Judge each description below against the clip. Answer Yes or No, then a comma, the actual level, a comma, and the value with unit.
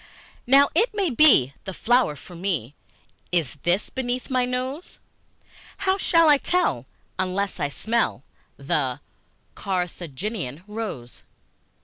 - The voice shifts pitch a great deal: Yes, wide, 7.4 semitones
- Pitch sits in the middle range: No, high, 210 Hz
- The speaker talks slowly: Yes, slow, 115 wpm